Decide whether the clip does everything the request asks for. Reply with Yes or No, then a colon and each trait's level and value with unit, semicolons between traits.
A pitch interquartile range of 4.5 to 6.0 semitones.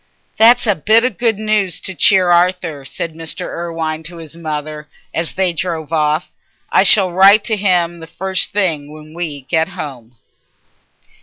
No: average, 3.5 semitones